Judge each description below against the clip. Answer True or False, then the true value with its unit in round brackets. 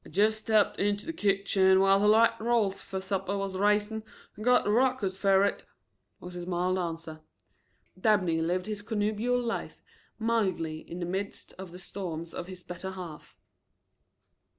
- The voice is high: True (195 Hz)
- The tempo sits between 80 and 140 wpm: False (165 wpm)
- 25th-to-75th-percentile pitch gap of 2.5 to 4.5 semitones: True (2.9 semitones)